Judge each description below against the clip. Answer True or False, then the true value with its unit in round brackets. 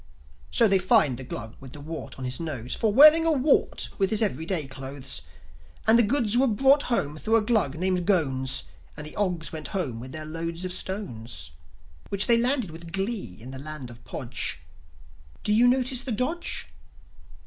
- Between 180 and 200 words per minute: True (190 wpm)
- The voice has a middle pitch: True (180 Hz)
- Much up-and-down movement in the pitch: True (8.9 semitones)